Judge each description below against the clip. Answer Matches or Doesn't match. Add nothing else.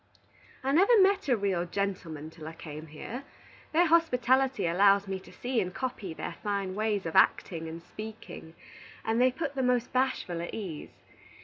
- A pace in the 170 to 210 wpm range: Matches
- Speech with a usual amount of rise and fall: Doesn't match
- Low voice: Doesn't match